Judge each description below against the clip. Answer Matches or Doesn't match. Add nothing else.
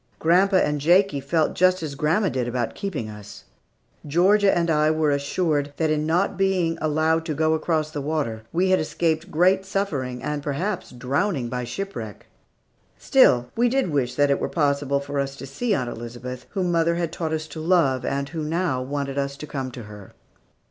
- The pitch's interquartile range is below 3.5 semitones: Doesn't match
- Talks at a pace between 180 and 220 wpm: Matches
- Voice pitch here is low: Doesn't match